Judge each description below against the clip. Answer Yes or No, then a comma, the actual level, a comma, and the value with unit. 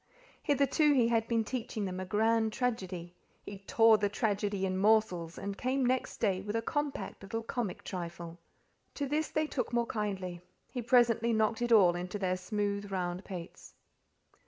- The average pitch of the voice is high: Yes, high, 210 Hz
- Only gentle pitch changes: No, average, 4.0 semitones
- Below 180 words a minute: Yes, average, 170 wpm